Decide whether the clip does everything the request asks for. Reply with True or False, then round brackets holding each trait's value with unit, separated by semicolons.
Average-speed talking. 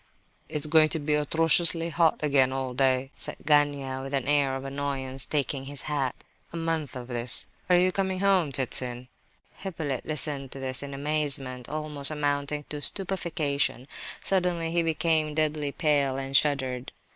True (155 wpm)